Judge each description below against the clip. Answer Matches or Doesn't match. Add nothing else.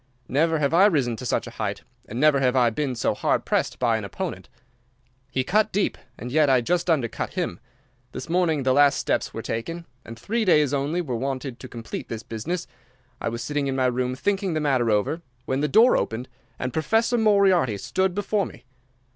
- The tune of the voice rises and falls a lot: Matches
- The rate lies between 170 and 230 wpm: Matches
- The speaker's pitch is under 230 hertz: Matches